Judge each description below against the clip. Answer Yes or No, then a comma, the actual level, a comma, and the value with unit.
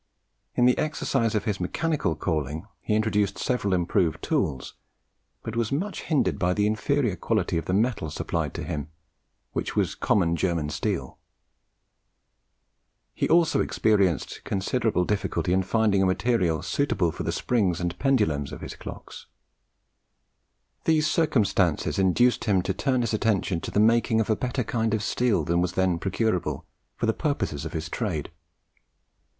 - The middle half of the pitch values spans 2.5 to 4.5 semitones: No, average, 5.0 semitones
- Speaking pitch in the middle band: No, low, 105 Hz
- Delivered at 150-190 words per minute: Yes, average, 155 wpm